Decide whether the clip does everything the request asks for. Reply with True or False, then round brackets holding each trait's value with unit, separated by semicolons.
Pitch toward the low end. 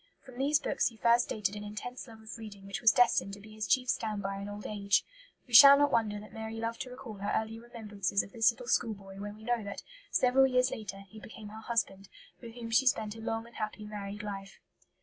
False (220 Hz)